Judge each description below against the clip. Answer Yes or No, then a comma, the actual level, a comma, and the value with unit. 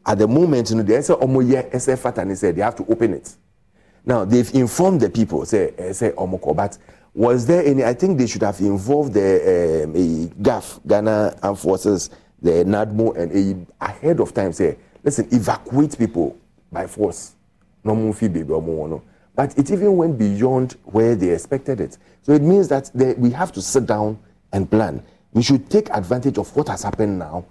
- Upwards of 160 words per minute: Yes, average, 185 wpm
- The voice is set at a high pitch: No, low, 115 Hz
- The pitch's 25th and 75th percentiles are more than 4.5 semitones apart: Yes, average, 5.0 semitones